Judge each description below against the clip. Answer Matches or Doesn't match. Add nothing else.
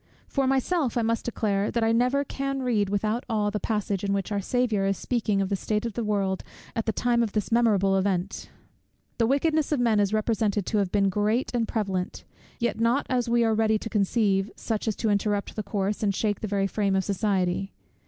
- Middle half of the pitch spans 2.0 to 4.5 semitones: Matches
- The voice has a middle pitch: Doesn't match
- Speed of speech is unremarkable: Doesn't match